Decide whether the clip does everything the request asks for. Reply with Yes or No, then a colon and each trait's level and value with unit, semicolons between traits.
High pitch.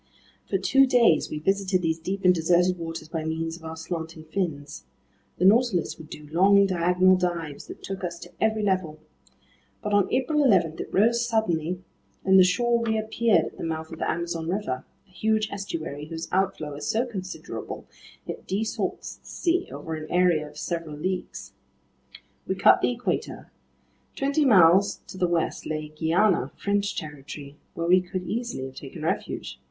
No: medium, 180 Hz